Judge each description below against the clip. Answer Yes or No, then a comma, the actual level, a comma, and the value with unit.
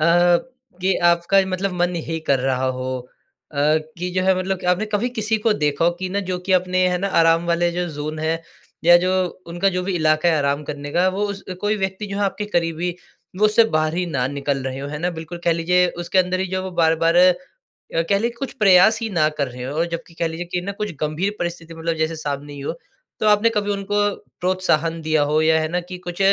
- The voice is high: No, medium, 175 Hz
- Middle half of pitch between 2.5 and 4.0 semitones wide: Yes, average, 3.1 semitones